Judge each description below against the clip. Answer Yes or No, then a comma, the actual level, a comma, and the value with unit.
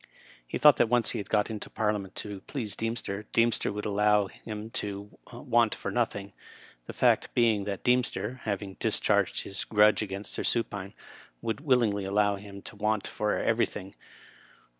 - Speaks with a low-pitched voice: Yes, low, 105 Hz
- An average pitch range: No, narrow, 2.1 semitones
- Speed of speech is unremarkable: Yes, average, 160 wpm